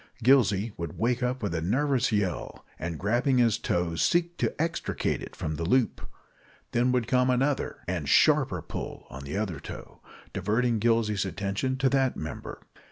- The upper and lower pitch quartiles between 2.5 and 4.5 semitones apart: No, wide, 5.5 semitones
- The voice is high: No, low, 115 Hz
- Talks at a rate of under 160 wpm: No, average, 165 wpm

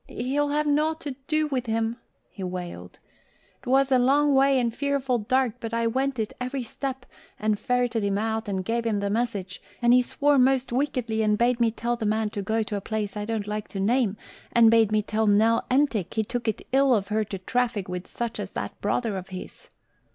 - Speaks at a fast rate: Yes, fast, 215 wpm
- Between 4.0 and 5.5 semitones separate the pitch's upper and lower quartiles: No, average, 3.5 semitones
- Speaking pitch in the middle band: No, high, 230 Hz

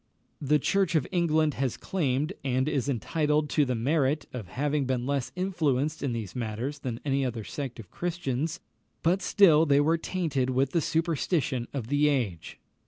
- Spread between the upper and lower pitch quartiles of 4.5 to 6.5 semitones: No, average, 3.8 semitones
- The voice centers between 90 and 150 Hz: Yes, medium, 140 Hz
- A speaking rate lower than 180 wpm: Yes, average, 170 wpm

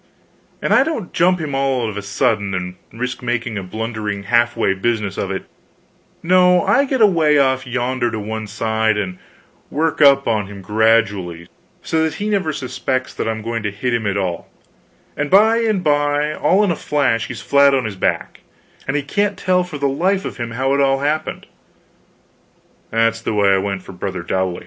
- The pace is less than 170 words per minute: No, average, 200 wpm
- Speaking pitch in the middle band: No, low, 120 Hz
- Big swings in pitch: Yes, wide, 6.1 semitones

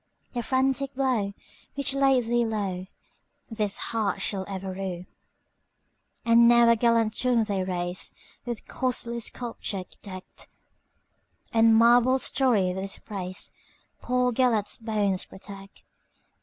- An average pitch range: Yes, average, 3.9 semitones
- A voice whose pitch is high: Yes, high, 225 Hz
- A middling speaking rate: No, slow, 100 wpm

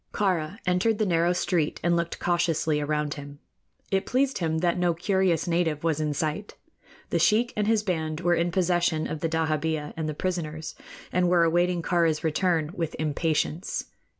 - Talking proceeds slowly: No, average, 175 wpm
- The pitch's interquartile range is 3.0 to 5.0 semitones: No, narrow, 2.4 semitones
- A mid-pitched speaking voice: Yes, medium, 170 Hz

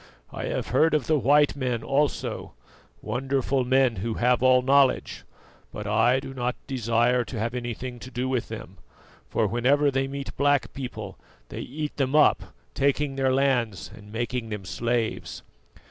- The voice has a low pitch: Yes, low, 130 Hz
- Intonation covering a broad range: No, narrow, 2.6 semitones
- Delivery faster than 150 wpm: Yes, average, 160 wpm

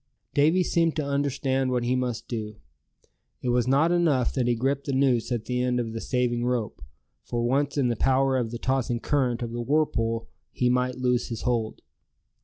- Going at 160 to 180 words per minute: No, average, 200 wpm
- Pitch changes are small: Yes, narrow, 2.3 semitones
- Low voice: Yes, low, 125 Hz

